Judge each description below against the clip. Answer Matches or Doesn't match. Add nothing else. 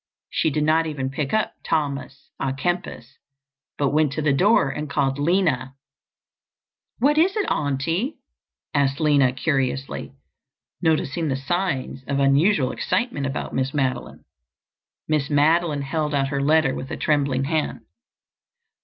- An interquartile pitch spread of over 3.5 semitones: Doesn't match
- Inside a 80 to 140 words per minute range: Matches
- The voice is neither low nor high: Matches